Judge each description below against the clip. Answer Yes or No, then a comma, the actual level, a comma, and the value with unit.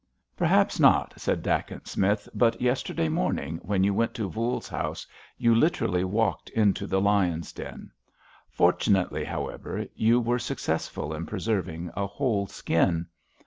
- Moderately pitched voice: No, low, 100 Hz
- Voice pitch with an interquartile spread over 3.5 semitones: Yes, average, 4.3 semitones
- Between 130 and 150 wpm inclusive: Yes, average, 140 wpm